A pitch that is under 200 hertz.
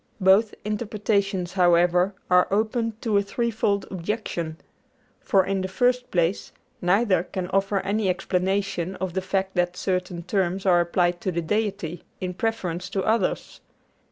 Yes: high, 190 Hz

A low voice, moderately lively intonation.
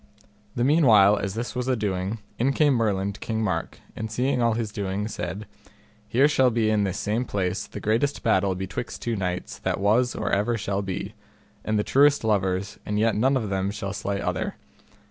Yes: low, 105 Hz; average, 3.3 semitones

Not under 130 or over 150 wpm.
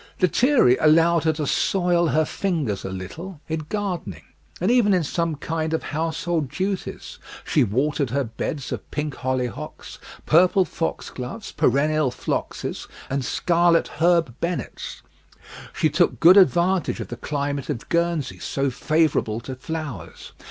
Yes: average, 140 wpm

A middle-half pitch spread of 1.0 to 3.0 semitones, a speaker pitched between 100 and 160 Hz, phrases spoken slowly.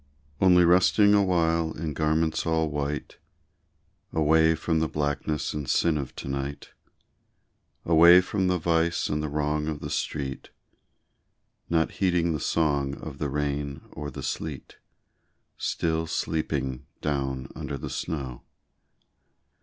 No: narrow, 2.4 semitones; very low, 80 Hz; slow, 130 wpm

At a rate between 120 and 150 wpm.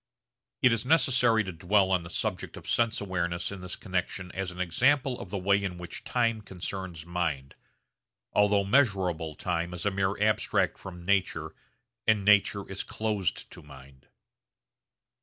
No: average, 160 wpm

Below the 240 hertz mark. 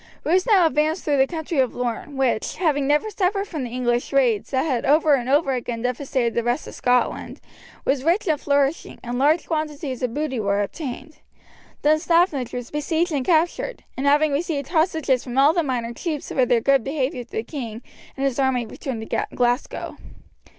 No: very high, 275 Hz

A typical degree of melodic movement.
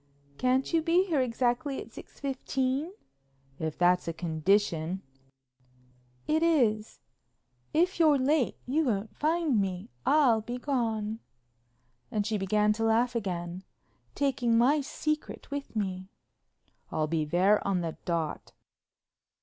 No: wide, 7.4 semitones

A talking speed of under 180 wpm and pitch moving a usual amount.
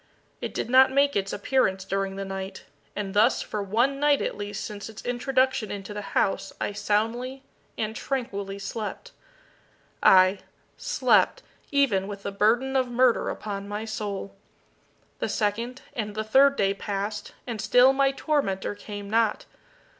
Yes: average, 155 wpm; average, 4.2 semitones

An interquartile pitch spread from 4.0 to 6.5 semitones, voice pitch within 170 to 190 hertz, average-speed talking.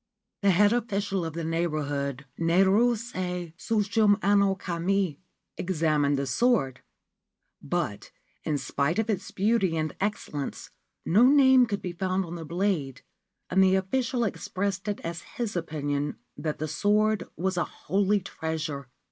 No: average, 4.5 semitones; medium, 185 Hz; slow, 130 wpm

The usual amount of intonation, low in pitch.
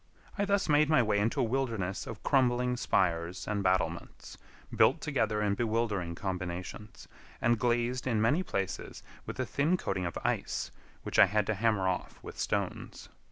Yes: average, 4.7 semitones; low, 110 Hz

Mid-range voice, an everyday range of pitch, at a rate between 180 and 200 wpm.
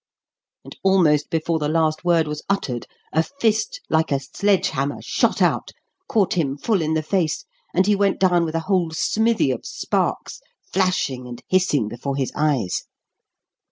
No: medium, 160 Hz; average, 4.7 semitones; average, 165 wpm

